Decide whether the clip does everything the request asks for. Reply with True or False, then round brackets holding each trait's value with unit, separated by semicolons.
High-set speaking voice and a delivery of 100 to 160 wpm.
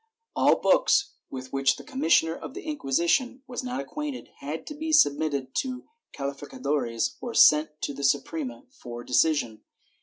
False (155 Hz; 150 wpm)